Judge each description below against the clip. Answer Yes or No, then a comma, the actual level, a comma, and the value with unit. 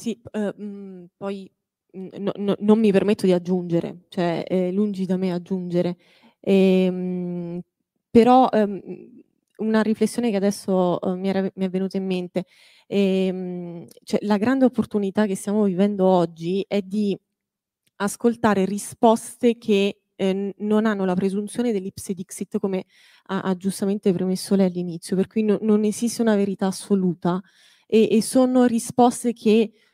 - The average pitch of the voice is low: No, high, 195 Hz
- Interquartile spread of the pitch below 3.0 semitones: Yes, narrow, 2.4 semitones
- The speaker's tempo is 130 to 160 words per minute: Yes, average, 145 wpm